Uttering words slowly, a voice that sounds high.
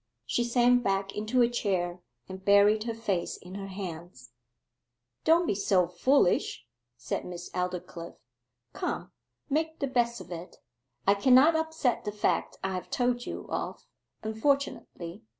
No: average, 145 wpm; high, 205 Hz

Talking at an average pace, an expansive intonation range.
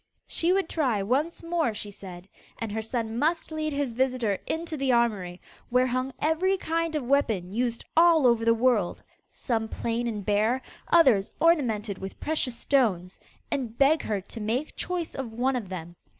Yes: average, 175 wpm; wide, 6.0 semitones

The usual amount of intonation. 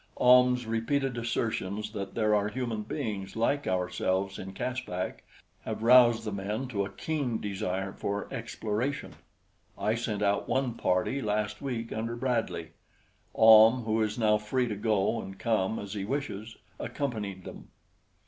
Yes: average, 3.2 semitones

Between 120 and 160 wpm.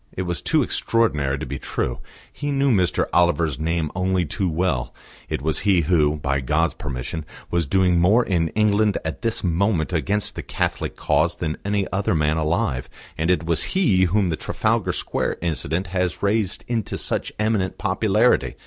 No: average, 175 wpm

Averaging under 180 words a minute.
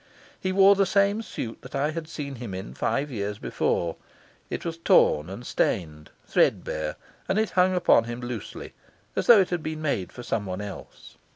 No: average, 185 wpm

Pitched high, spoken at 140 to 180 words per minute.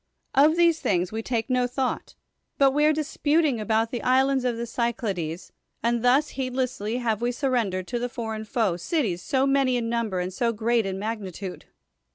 No: high, 235 Hz; average, 195 wpm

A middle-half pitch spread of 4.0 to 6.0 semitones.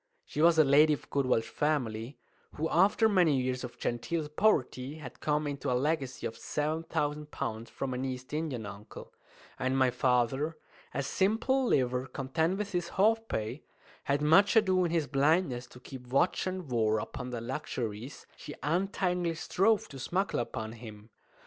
Yes: average, 5.1 semitones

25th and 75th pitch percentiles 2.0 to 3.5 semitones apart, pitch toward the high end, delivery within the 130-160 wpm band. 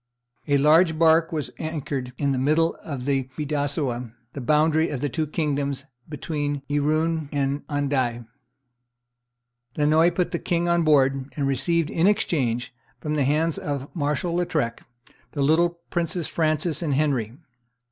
No: average, 2.7 semitones; medium, 150 Hz; average, 145 wpm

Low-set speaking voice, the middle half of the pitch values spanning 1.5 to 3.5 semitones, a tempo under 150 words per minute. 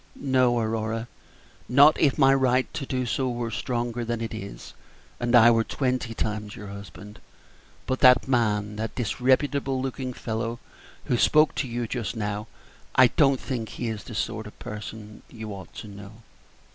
No: low, 115 Hz; average, 3.0 semitones; average, 170 wpm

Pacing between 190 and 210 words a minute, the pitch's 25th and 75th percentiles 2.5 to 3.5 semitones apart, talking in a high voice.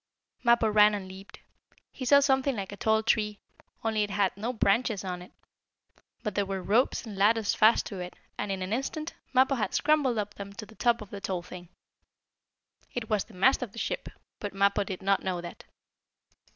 Yes: fast, 205 wpm; average, 3.2 semitones; high, 210 Hz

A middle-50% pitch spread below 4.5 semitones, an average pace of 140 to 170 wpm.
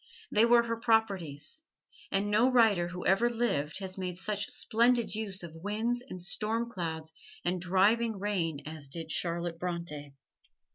No: average, 4.9 semitones; average, 150 wpm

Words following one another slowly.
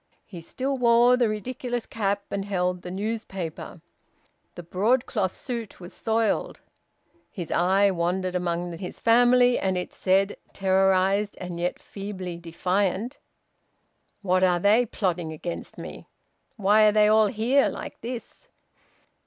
Yes: slow, 130 wpm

